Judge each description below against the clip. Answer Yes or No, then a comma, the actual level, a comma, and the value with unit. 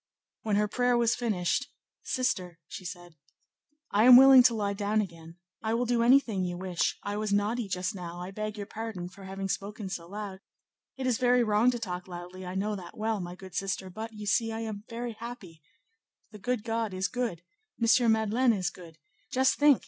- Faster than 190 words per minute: Yes, average, 200 wpm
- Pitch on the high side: Yes, high, 210 Hz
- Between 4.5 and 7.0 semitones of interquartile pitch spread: No, average, 3.8 semitones